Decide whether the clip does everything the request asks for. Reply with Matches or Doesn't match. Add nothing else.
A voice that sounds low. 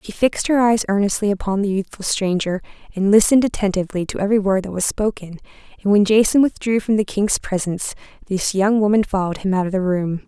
Doesn't match